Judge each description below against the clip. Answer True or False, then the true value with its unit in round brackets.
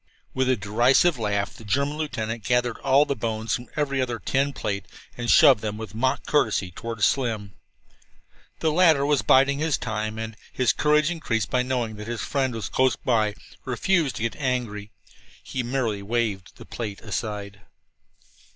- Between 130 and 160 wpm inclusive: False (170 wpm)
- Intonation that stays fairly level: False (4.1 semitones)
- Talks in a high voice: False (120 Hz)